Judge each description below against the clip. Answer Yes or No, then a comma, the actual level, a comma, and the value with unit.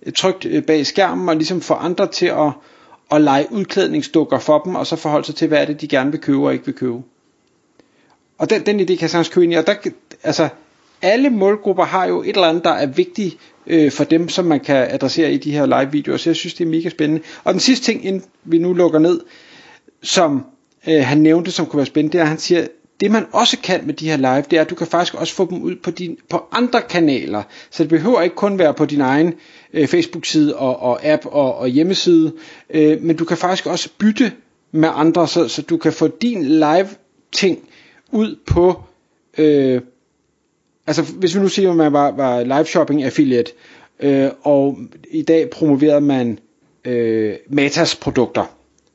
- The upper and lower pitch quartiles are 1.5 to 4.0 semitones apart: Yes, average, 3.4 semitones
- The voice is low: No, medium, 165 Hz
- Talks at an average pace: Yes, average, 210 wpm